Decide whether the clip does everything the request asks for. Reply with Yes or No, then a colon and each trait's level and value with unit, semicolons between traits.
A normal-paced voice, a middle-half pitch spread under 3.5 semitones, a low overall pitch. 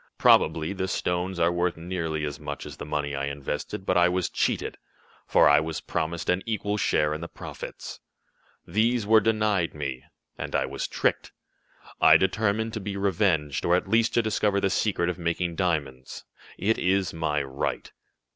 No: average, 175 wpm; average, 4.3 semitones; very low, 90 Hz